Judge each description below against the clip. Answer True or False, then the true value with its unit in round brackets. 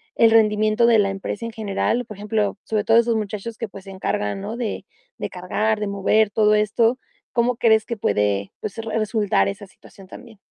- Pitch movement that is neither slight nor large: False (2.2 semitones)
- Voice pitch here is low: False (215 Hz)